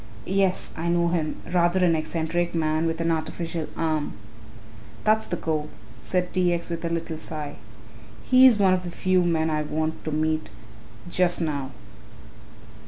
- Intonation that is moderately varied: No, narrow, 2.1 semitones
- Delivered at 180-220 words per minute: No, average, 160 wpm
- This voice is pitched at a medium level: Yes, medium, 165 Hz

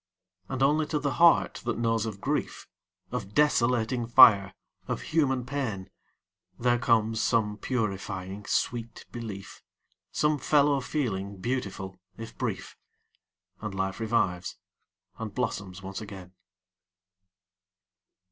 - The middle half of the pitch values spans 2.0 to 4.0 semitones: No, average, 4.7 semitones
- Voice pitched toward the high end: No, low, 115 Hz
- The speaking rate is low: Yes, slow, 110 wpm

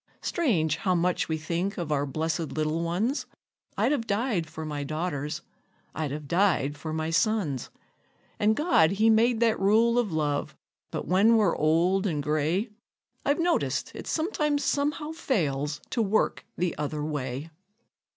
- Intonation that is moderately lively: No, wide, 6.4 semitones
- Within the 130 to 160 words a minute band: Yes, average, 155 wpm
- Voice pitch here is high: No, medium, 175 Hz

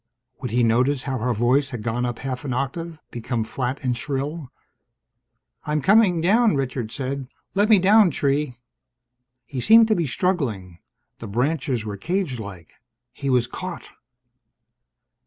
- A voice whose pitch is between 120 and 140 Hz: Yes, low, 135 Hz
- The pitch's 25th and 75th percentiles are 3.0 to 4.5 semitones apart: No, wide, 5.4 semitones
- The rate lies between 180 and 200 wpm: No, average, 145 wpm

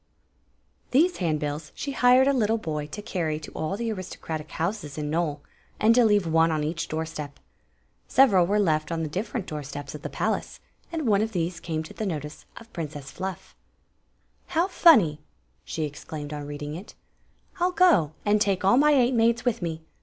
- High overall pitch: No, medium, 175 Hz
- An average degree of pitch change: No, wide, 6.6 semitones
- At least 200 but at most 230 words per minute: Yes, fast, 205 wpm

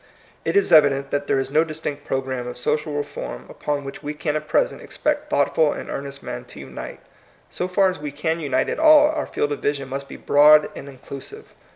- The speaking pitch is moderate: Yes, medium, 145 Hz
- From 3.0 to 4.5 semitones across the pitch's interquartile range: No, narrow, 2.5 semitones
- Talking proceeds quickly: Yes, fast, 220 wpm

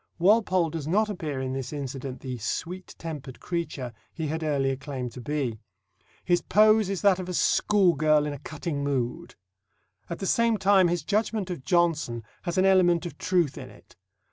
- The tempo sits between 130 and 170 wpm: No, average, 180 wpm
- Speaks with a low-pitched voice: No, medium, 165 Hz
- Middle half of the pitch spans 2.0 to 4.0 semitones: No, average, 5.2 semitones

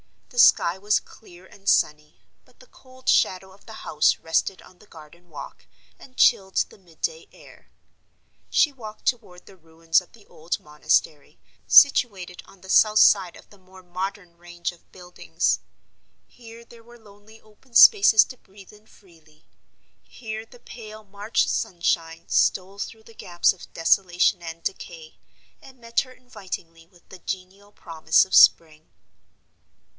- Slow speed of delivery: No, average, 155 wpm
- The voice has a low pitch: No, high, 190 Hz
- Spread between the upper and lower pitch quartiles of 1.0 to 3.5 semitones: No, average, 4.2 semitones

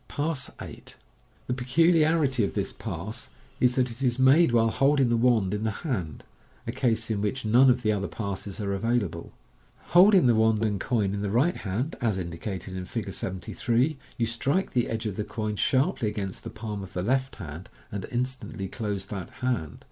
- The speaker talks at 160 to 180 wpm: No, average, 195 wpm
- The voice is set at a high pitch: No, low, 115 Hz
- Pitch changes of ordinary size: Yes, average, 4.3 semitones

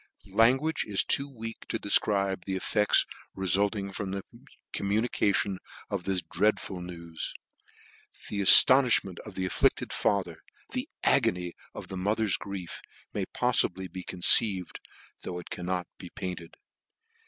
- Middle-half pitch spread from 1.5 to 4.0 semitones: Yes, narrow, 2.5 semitones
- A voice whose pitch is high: No, very low, 95 Hz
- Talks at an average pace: No, slow, 130 wpm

